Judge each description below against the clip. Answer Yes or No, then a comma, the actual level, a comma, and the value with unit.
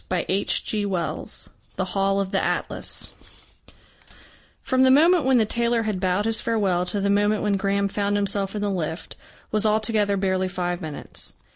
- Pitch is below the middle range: No, high, 200 Hz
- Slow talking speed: No, average, 165 wpm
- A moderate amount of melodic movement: No, narrow, 2.3 semitones